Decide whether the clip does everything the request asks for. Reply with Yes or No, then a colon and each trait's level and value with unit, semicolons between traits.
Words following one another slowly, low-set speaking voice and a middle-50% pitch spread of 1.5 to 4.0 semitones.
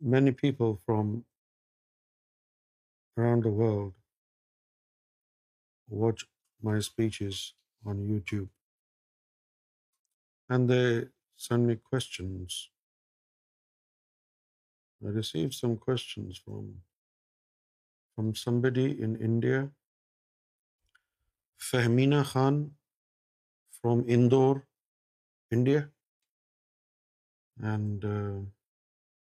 Yes: slow, 60 wpm; low, 115 Hz; average, 3.7 semitones